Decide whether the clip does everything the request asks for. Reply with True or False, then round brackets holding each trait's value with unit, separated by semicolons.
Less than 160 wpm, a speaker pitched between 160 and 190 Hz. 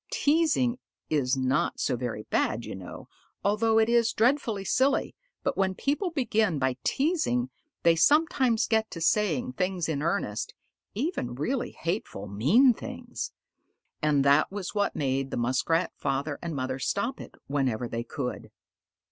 True (150 wpm; 185 Hz)